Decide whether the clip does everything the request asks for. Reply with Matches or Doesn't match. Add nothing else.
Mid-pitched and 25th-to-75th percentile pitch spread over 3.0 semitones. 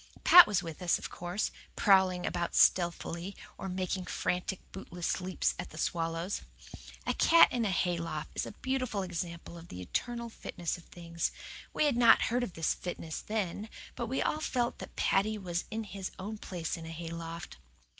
Matches